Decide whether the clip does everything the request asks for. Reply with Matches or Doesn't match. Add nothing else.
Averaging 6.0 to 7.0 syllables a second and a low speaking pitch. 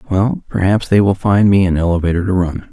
Doesn't match